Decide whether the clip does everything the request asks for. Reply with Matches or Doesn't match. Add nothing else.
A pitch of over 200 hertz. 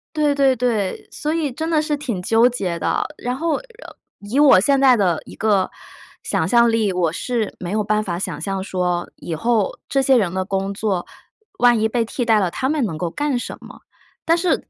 Matches